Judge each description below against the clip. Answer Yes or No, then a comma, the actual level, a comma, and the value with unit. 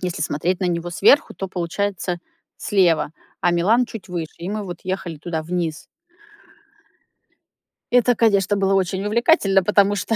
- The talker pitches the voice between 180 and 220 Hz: Yes, high, 190 Hz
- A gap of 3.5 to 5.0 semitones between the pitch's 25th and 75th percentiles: No, average, 2.9 semitones